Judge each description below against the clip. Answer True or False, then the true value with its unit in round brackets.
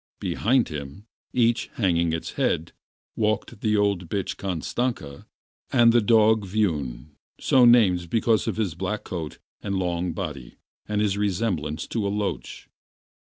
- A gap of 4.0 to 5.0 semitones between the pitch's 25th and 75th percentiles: True (4.5 semitones)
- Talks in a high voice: False (100 Hz)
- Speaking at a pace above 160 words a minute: False (140 wpm)